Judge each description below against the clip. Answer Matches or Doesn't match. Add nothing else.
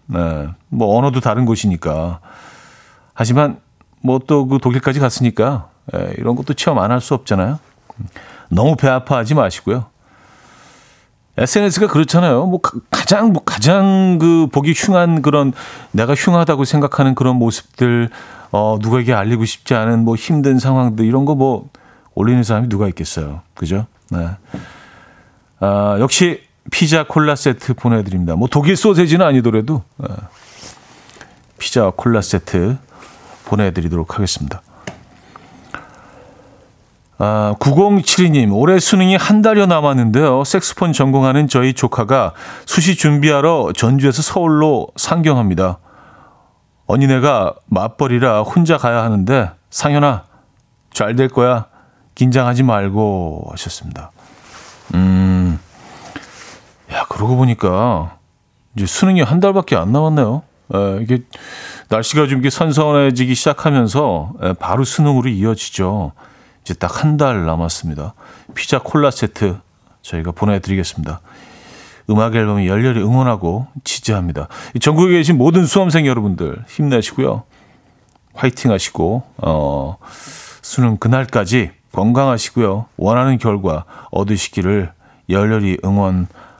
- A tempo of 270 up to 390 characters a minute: Matches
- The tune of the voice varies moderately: Doesn't match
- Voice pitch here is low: Matches